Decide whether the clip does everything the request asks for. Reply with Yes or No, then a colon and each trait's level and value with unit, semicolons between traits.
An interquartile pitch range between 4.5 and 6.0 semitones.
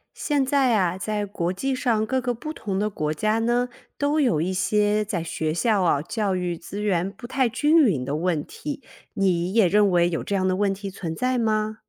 Yes: average, 4.9 semitones